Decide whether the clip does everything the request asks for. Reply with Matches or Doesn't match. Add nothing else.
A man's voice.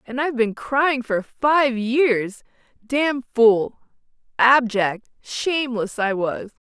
Doesn't match